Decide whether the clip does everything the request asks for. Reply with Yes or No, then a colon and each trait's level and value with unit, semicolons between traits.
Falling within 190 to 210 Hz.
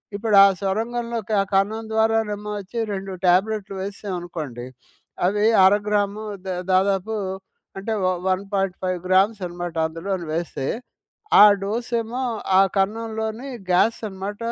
Yes: high, 200 Hz